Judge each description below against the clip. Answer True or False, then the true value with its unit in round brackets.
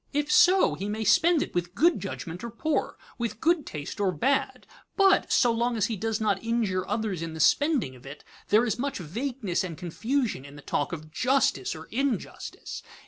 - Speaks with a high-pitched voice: True (220 Hz)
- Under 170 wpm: False (195 wpm)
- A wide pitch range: True (7.3 semitones)